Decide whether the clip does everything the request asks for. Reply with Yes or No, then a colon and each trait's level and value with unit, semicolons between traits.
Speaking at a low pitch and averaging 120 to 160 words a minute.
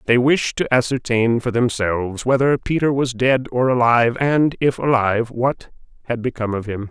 No: low, 120 Hz; average, 175 wpm